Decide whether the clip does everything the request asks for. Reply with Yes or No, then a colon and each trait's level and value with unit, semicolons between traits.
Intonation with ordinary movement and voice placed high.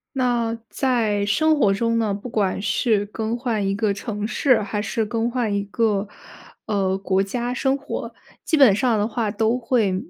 Yes: average, 3.1 semitones; high, 220 Hz